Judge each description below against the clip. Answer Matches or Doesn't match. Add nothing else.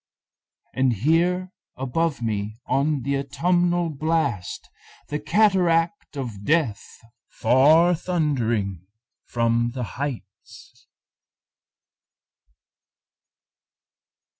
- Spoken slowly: Matches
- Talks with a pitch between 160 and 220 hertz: Doesn't match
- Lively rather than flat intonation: Matches